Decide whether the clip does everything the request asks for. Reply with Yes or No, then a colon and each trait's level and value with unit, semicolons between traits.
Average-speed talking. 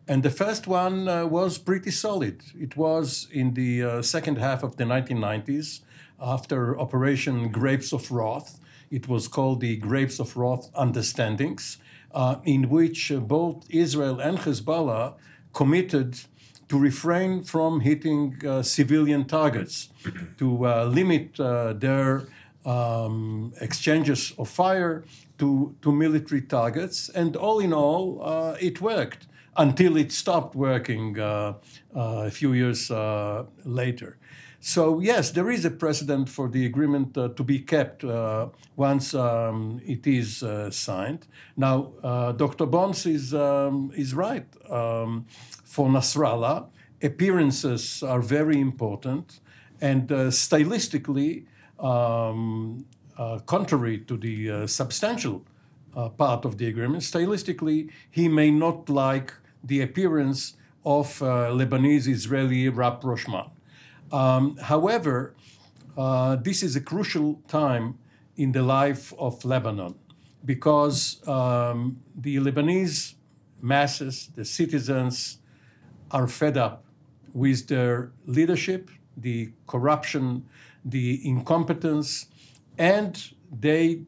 No: slow, 120 wpm